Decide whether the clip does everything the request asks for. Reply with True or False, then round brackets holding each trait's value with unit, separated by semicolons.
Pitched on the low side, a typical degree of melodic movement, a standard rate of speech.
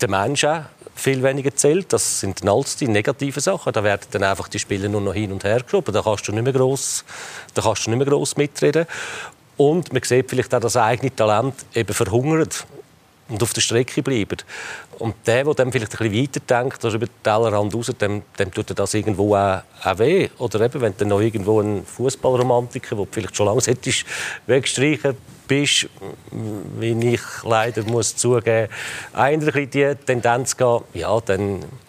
True (120 Hz; 4.2 semitones; 175 wpm)